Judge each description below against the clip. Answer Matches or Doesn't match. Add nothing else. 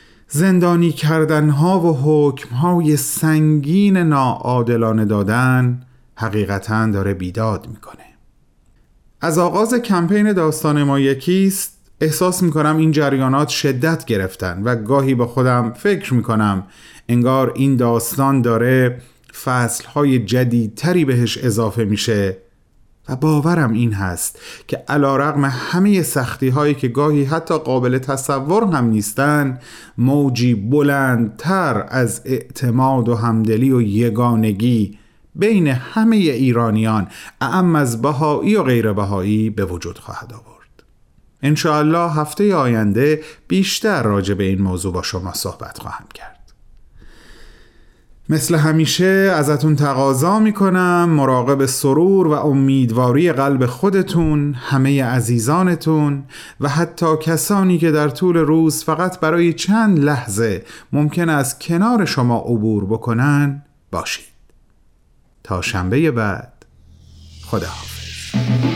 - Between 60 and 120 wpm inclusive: Matches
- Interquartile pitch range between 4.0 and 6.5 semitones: Matches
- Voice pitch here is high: Doesn't match